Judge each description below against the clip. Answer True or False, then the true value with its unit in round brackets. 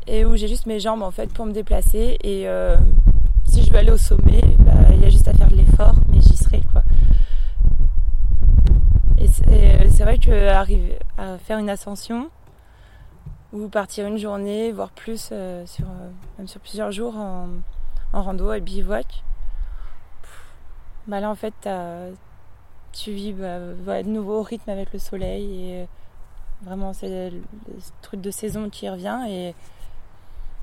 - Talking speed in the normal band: True (170 wpm)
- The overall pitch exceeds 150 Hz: True (185 Hz)